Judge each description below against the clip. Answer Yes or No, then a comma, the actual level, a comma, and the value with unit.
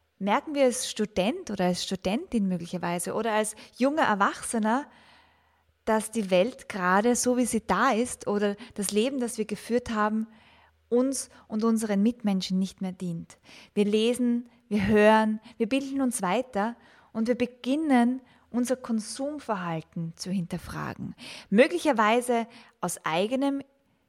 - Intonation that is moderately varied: Yes, average, 3.3 semitones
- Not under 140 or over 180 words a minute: No, average, 130 wpm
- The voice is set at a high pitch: Yes, high, 225 Hz